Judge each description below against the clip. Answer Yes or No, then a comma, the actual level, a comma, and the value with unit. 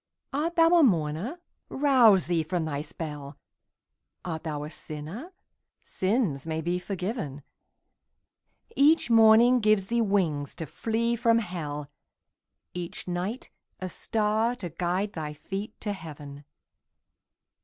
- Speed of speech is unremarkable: No, slow, 120 wpm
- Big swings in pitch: Yes, wide, 6.5 semitones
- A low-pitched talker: No, medium, 185 Hz